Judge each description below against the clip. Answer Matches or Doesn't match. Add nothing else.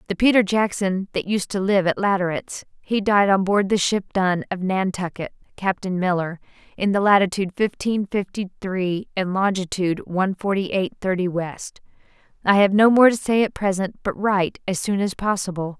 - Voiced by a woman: Matches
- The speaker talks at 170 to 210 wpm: Matches